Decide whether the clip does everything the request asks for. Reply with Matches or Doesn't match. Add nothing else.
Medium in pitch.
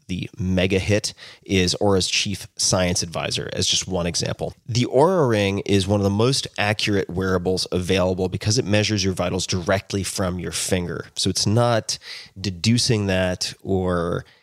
Doesn't match